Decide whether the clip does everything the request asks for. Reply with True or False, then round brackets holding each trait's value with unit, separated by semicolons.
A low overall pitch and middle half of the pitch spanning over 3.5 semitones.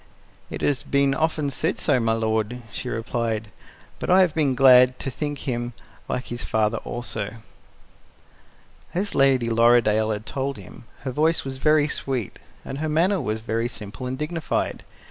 True (125 Hz; 4.2 semitones)